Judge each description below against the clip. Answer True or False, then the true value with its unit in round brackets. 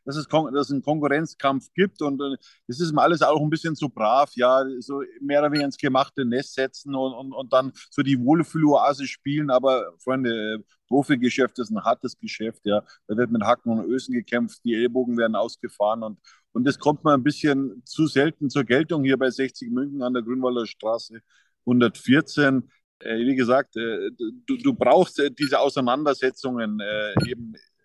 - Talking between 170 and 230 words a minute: True (185 wpm)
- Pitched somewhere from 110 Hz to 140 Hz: True (135 Hz)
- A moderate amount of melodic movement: True (3.2 semitones)